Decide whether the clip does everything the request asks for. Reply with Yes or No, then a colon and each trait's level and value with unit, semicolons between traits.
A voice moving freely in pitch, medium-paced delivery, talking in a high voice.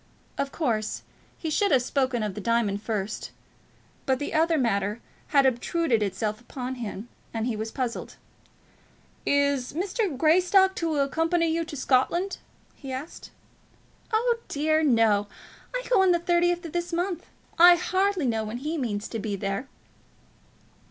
Yes: wide, 7.0 semitones; average, 150 wpm; very high, 275 Hz